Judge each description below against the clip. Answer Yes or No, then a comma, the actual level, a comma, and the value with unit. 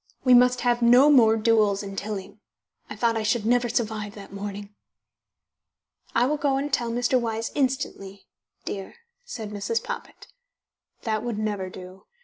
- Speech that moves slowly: No, average, 155 wpm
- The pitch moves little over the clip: No, average, 3.1 semitones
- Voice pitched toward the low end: No, high, 225 Hz